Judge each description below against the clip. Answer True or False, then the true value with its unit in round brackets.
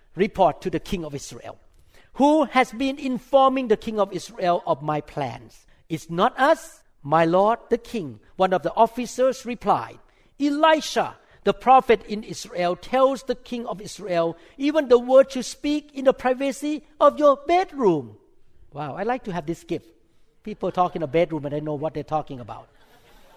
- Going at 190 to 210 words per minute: False (175 wpm)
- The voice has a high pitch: True (210 Hz)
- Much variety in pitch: True (8.1 semitones)